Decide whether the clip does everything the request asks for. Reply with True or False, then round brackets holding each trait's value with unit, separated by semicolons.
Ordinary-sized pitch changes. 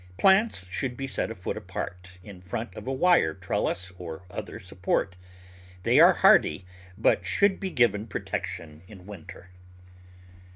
False (5.8 semitones)